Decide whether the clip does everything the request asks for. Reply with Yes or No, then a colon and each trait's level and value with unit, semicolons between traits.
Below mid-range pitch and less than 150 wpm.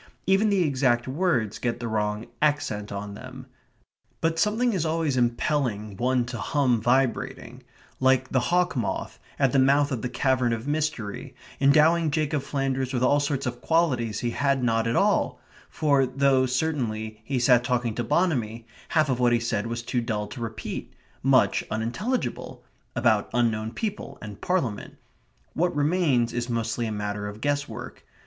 No: low, 130 Hz; average, 165 wpm